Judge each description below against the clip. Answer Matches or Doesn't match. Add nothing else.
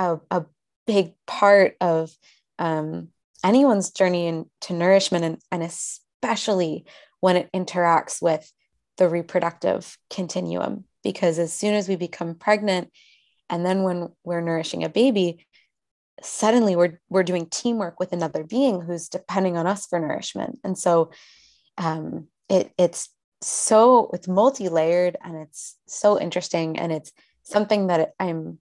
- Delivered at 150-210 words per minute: Doesn't match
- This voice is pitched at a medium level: Matches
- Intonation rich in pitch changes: Doesn't match